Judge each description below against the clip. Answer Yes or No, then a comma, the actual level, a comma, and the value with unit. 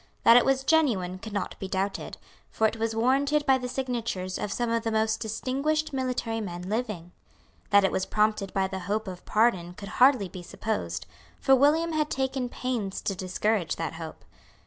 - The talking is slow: No, average, 190 wpm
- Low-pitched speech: No, high, 220 Hz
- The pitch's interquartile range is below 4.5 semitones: No, average, 5.1 semitones